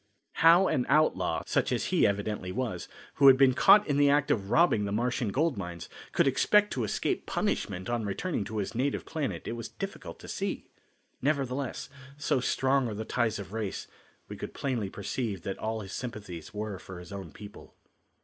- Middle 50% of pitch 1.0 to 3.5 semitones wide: No, average, 5.3 semitones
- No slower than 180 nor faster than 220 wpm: Yes, average, 190 wpm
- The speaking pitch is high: No, low, 115 Hz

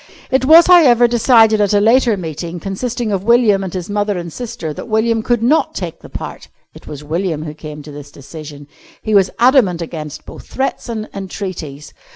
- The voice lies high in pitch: Yes, high, 200 Hz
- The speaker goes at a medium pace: Yes, average, 195 wpm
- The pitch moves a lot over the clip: Yes, wide, 6.3 semitones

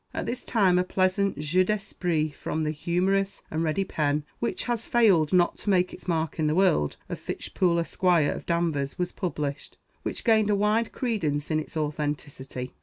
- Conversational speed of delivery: Yes, average, 185 wpm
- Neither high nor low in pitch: Yes, medium, 175 Hz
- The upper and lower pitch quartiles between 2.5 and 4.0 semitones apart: No, average, 4.4 semitones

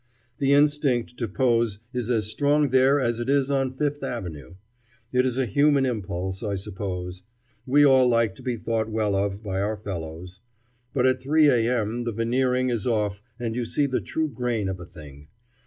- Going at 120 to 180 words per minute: No, average, 190 wpm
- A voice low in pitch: Yes, low, 120 Hz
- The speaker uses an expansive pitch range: No, average, 4.6 semitones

